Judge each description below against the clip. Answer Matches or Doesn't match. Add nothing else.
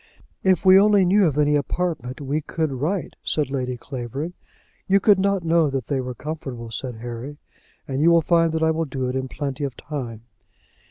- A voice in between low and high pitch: Matches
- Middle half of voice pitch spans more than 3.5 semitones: Matches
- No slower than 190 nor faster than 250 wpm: Matches